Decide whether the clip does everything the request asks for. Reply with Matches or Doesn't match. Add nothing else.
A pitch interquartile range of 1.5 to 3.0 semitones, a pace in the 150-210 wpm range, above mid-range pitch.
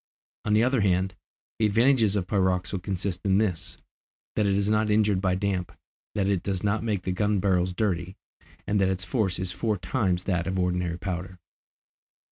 Doesn't match